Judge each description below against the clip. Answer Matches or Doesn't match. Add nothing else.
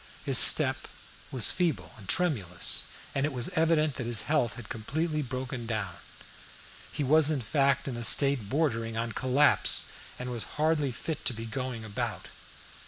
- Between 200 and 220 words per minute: Doesn't match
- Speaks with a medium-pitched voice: Doesn't match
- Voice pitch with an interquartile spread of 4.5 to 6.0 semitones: Matches